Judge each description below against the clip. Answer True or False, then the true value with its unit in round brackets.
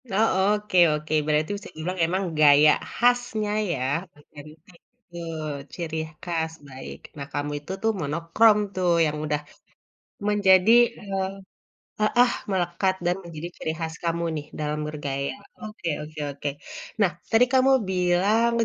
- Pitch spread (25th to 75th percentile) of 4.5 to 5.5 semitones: True (5.2 semitones)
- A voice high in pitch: False (170 Hz)